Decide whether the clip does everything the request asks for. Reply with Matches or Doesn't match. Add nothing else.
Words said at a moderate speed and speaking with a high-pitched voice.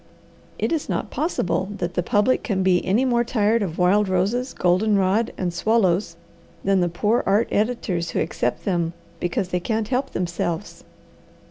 Matches